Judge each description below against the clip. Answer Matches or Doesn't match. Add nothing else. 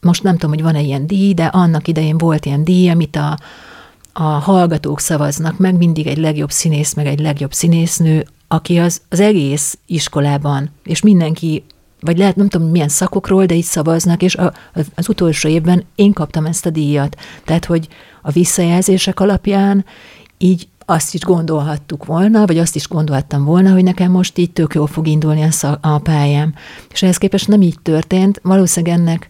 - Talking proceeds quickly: Matches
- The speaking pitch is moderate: Matches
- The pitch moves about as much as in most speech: Matches